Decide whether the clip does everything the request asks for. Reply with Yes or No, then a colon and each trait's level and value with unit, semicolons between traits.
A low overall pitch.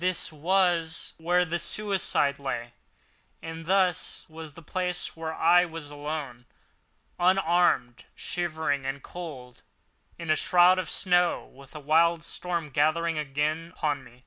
No: medium, 165 Hz